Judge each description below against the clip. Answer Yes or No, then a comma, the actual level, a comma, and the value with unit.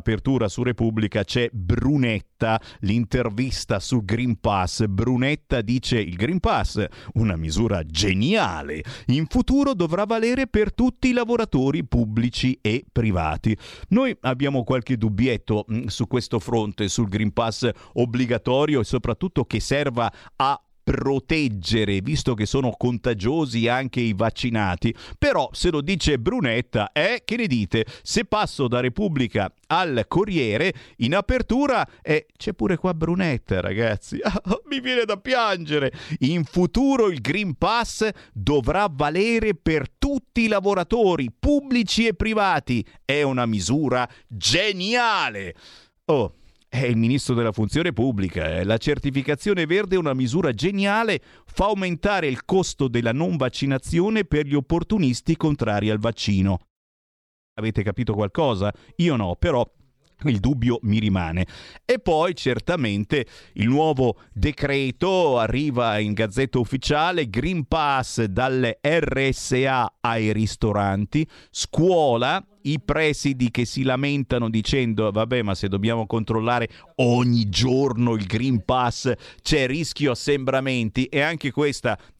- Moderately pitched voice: No, low, 130 Hz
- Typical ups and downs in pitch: No, wide, 6.1 semitones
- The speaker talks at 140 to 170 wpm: No, average, 125 wpm